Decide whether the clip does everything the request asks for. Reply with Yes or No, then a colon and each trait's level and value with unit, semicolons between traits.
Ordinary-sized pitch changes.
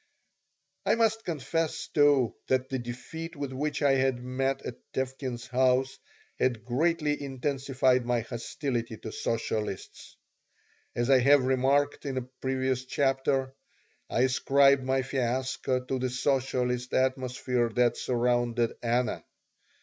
No: narrow, 1.7 semitones